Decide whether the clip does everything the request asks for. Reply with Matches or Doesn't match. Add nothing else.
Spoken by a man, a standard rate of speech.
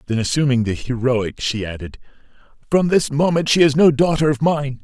Matches